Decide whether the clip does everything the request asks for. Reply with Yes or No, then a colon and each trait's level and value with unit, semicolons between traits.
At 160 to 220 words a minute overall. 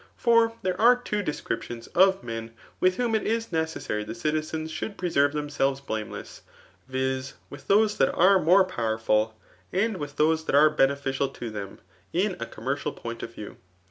Yes: average, 175 wpm